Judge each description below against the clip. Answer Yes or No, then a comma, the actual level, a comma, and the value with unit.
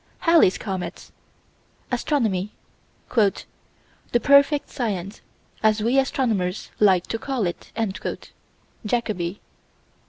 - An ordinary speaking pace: No, slow, 85 wpm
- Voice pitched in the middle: No, high, 215 Hz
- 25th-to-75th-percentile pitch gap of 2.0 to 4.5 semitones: No, average, 5.2 semitones